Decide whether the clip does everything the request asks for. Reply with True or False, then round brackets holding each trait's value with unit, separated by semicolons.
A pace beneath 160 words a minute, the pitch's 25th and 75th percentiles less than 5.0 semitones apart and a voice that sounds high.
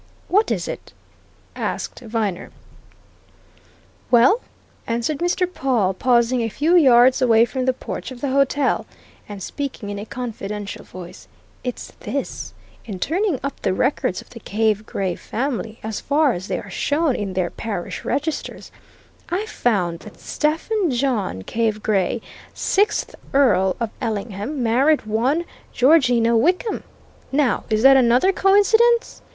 False (140 wpm; 5.3 semitones; 245 Hz)